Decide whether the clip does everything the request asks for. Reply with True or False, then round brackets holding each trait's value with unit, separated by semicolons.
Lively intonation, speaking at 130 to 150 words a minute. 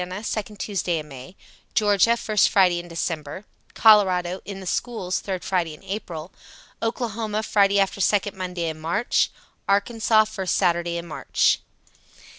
False (3.4 semitones; 140 wpm)